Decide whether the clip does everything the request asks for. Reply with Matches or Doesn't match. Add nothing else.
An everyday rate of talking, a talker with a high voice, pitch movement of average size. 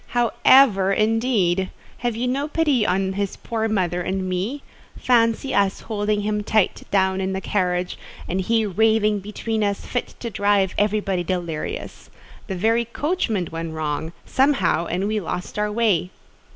Matches